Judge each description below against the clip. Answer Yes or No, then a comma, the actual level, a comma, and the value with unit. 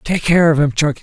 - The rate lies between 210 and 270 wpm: No, fast, 290 wpm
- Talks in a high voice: No, medium, 155 Hz